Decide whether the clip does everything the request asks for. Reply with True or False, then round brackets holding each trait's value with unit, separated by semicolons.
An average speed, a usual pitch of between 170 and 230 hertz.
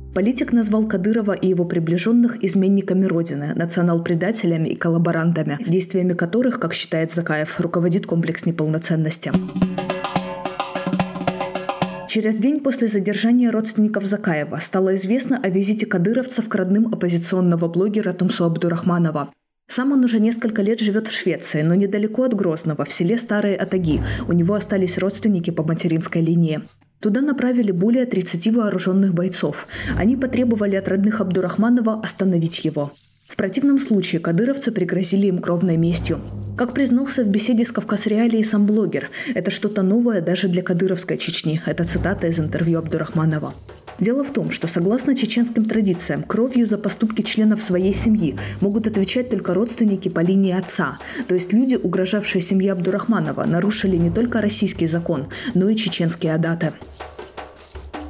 True (140 wpm; 190 Hz)